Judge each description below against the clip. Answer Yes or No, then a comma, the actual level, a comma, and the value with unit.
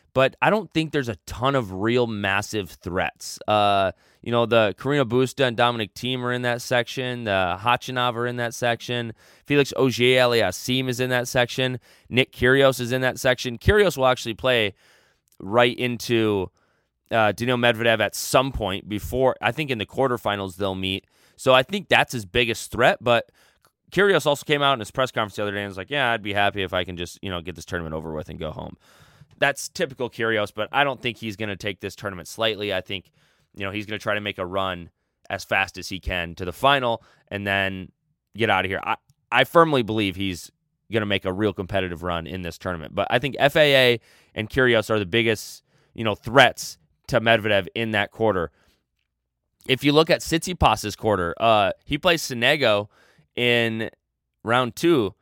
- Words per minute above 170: Yes, average, 200 wpm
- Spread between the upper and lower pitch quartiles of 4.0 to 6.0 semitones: Yes, average, 4.7 semitones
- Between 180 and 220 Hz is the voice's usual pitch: No, low, 115 Hz